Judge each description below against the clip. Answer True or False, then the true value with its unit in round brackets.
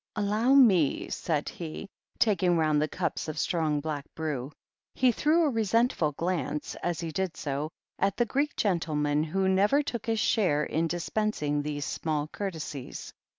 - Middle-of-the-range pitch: True (170 Hz)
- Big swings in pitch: True (5.7 semitones)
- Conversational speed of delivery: True (155 wpm)